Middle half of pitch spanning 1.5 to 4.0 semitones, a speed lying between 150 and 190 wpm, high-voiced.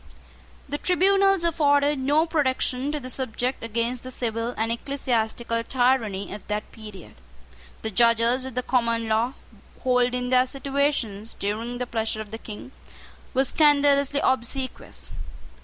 No: average, 3.5 semitones; slow, 135 wpm; very high, 250 Hz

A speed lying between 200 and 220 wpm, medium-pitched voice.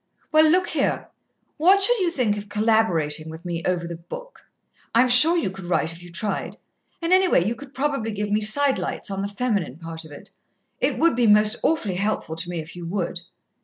No: fast, 205 wpm; high, 210 Hz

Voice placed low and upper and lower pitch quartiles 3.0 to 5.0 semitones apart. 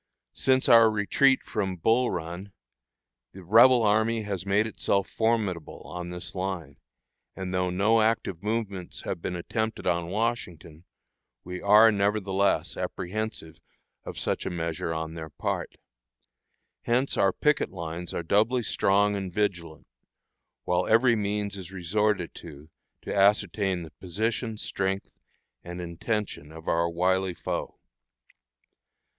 Yes: very low, 95 Hz; average, 3.8 semitones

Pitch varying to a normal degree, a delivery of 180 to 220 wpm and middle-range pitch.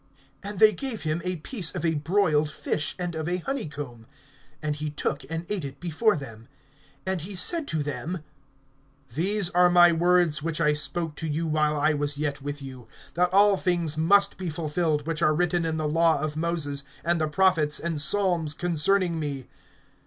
Yes: average, 3.0 semitones; average, 190 wpm; medium, 160 Hz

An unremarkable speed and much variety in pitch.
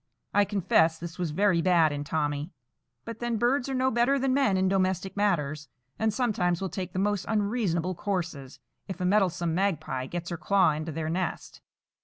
No: average, 185 wpm; average, 4.1 semitones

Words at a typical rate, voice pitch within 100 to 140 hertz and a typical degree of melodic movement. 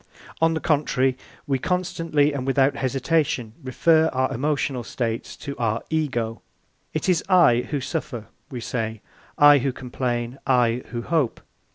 Yes: average, 145 wpm; low, 135 Hz; average, 4.0 semitones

